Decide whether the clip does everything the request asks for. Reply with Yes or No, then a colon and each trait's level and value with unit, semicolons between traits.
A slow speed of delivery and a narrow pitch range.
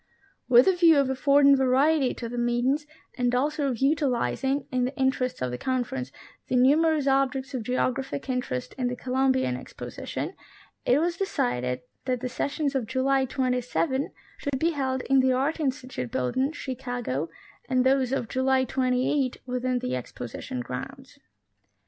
No: average, 155 wpm; narrow, 1.8 semitones